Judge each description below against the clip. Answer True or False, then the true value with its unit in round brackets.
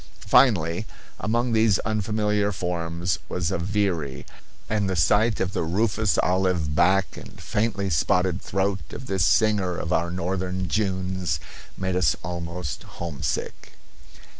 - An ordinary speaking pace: False (130 wpm)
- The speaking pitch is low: True (95 Hz)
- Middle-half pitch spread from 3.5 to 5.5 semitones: False (3.1 semitones)